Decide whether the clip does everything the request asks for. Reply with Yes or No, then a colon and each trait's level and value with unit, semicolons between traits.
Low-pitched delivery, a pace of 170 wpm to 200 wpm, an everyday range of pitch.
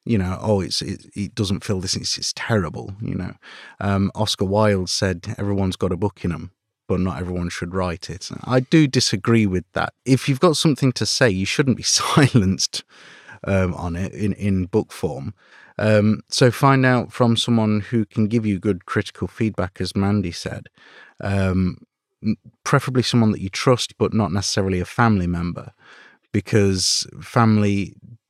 Yes: low, 105 Hz; average, 175 wpm; average, 3.6 semitones